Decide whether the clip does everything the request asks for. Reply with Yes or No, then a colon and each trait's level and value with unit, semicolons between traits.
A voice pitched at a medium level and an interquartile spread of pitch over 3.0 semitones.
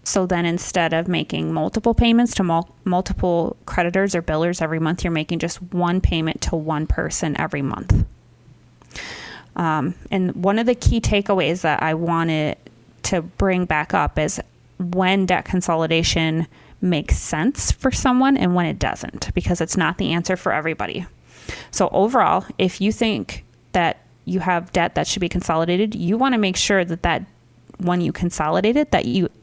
No: medium, 175 Hz; average, 2.7 semitones